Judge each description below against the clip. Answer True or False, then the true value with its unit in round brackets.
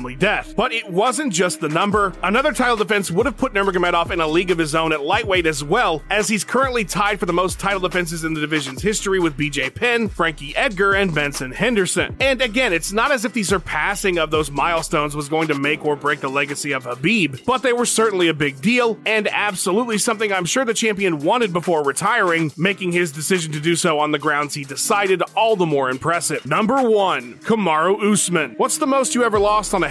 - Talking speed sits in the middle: False (225 wpm)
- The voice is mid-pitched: True (180 Hz)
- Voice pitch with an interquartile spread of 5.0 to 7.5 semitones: True (5.4 semitones)